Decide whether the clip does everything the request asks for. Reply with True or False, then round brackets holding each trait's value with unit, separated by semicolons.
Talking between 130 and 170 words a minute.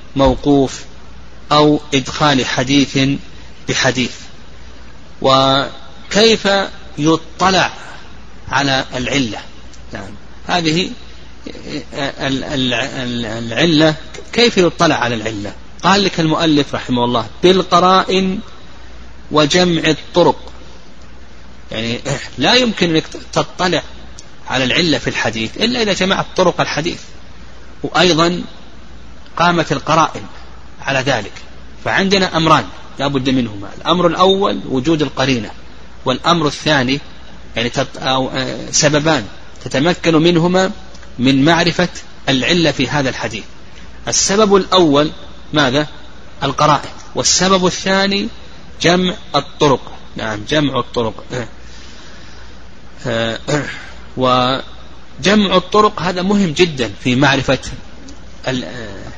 False (85 wpm)